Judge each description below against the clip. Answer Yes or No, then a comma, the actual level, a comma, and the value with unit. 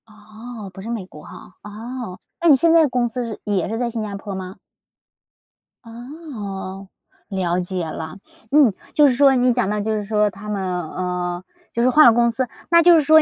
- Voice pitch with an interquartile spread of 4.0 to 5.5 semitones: Yes, average, 4.7 semitones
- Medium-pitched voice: No, high, 220 Hz